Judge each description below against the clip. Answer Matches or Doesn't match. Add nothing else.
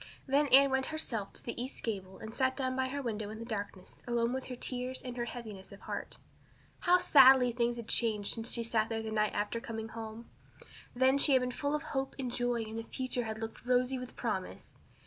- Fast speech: Matches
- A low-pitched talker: Doesn't match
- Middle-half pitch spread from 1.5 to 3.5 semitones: Matches